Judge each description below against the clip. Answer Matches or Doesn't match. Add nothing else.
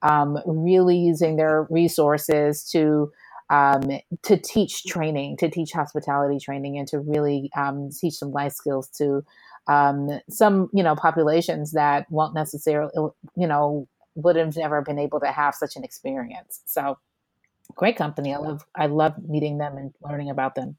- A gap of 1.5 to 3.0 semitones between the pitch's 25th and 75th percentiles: Matches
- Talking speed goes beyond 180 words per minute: Doesn't match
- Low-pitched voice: Doesn't match